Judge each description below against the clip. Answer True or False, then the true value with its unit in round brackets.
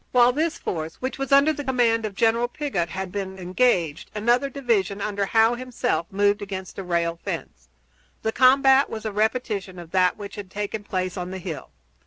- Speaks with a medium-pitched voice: False (205 Hz)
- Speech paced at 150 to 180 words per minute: False (190 wpm)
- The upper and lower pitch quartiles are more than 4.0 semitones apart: True (4.8 semitones)